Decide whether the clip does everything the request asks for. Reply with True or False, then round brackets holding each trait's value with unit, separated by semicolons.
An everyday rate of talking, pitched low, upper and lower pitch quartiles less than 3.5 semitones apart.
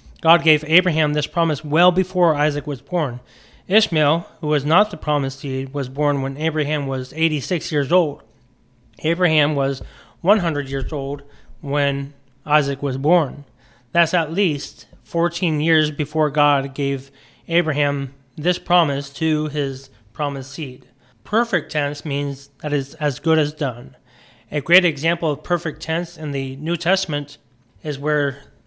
False (145 wpm; 150 Hz; 2.9 semitones)